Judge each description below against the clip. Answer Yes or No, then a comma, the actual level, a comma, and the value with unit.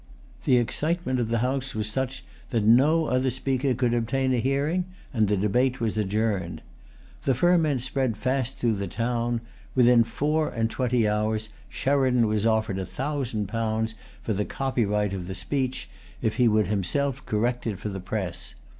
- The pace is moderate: Yes, average, 170 wpm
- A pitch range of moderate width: Yes, average, 3.6 semitones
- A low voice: Yes, low, 120 Hz